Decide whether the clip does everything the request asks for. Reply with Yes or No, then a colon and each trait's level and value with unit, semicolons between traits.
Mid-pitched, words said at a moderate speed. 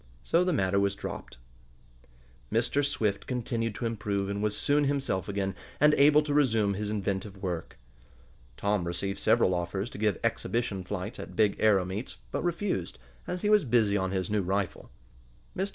No: low, 105 Hz; average, 170 wpm